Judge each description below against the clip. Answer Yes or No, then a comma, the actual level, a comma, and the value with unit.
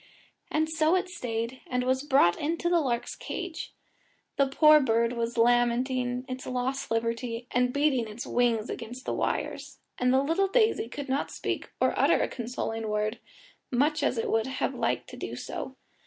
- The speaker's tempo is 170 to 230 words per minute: Yes, average, 175 wpm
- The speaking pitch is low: No, very high, 250 Hz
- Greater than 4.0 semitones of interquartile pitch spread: No, average, 3.7 semitones